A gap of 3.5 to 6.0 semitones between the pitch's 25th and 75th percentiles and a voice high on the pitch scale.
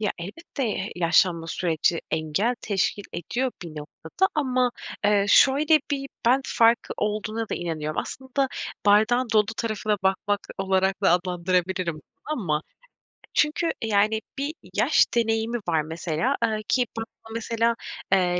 Yes: average, 5.1 semitones; high, 210 Hz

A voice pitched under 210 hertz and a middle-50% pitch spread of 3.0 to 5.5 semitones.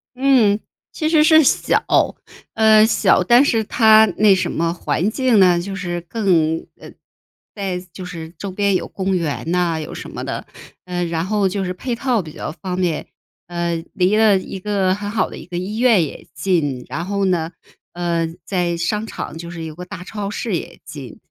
Yes: medium, 185 Hz; average, 3.7 semitones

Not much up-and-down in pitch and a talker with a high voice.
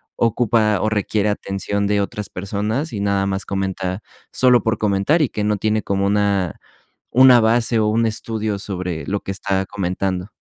No: narrow, 2.1 semitones; low, 105 Hz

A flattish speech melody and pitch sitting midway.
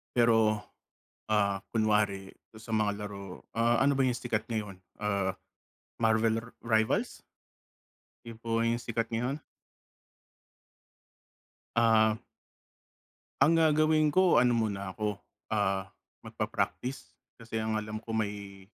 No: narrow, 2.1 semitones; low, 110 Hz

